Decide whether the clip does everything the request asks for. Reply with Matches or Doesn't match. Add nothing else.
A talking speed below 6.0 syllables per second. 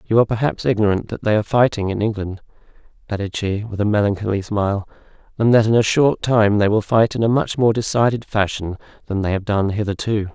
Doesn't match